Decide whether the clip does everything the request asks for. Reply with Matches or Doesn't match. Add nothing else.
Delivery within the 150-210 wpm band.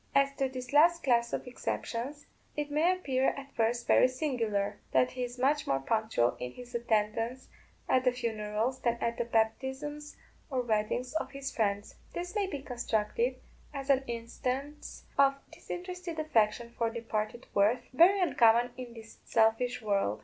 Matches